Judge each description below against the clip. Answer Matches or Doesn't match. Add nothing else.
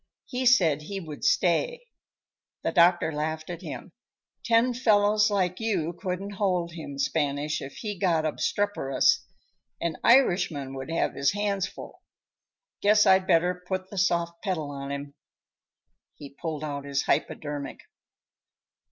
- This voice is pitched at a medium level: Matches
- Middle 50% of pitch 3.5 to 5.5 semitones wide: Matches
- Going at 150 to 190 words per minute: Doesn't match